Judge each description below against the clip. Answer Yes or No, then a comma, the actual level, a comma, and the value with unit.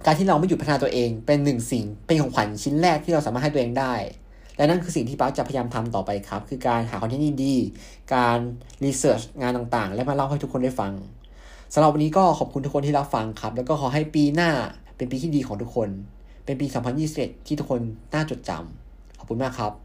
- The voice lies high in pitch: No, low, 130 Hz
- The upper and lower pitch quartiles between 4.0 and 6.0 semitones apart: Yes, average, 4.5 semitones